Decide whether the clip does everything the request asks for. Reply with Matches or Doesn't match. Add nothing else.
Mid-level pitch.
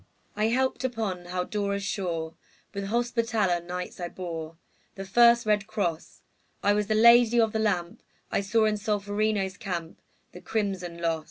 Doesn't match